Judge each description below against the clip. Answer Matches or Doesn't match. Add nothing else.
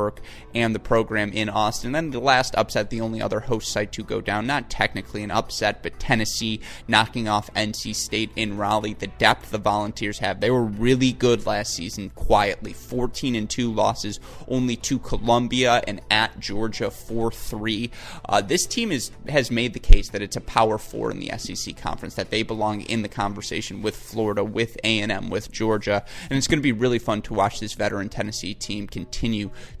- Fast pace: Doesn't match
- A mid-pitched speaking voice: Doesn't match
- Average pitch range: Doesn't match